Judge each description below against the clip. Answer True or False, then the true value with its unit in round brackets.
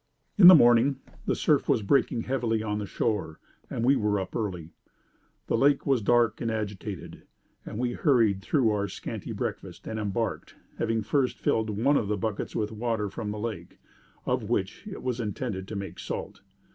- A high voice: False (110 Hz)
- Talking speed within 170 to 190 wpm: True (185 wpm)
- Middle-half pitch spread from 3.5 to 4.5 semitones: False (2.7 semitones)